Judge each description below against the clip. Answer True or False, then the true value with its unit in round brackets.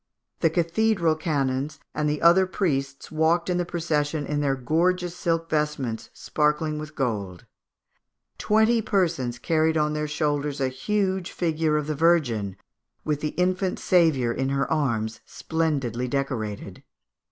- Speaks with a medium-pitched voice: True (150 Hz)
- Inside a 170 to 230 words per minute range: False (140 wpm)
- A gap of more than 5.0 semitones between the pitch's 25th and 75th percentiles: False (3.6 semitones)